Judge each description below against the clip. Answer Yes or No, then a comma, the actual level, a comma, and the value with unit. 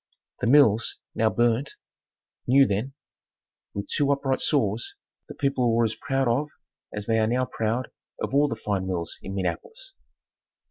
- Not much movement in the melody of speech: No, average, 4.3 semitones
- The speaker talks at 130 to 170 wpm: Yes, average, 155 wpm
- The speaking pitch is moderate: No, low, 120 Hz